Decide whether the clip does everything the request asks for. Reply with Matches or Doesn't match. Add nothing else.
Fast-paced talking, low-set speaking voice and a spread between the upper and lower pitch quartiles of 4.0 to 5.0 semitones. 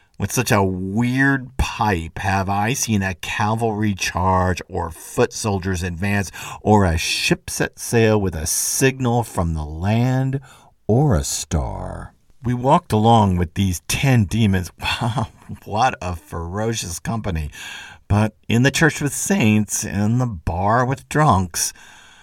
Doesn't match